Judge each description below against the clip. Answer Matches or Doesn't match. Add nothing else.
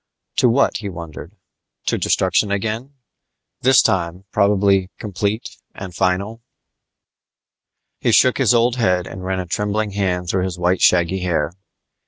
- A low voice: Matches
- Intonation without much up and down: Doesn't match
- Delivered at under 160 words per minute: Matches